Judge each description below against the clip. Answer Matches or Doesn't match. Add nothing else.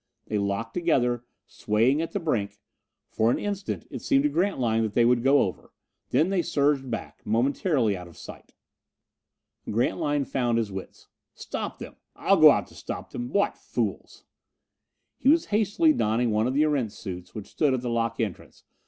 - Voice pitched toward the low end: Matches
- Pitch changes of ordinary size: Doesn't match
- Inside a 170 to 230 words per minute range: Matches